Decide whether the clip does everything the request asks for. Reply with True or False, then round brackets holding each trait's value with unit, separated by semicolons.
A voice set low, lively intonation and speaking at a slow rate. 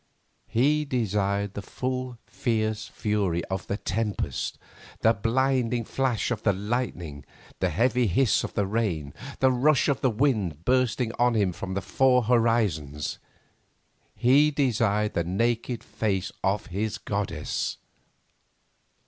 False (110 Hz; 4.1 semitones; 130 wpm)